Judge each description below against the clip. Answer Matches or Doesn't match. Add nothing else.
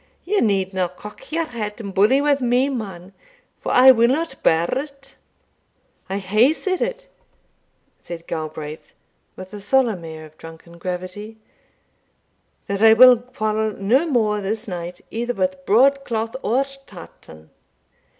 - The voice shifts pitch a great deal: Matches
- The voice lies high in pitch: Matches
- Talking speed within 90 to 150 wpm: Matches